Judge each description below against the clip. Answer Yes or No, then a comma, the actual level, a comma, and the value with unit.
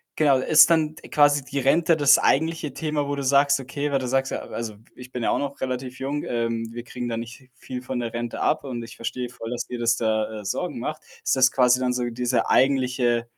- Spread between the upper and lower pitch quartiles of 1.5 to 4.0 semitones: Yes, average, 2.9 semitones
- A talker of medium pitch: No, low, 130 Hz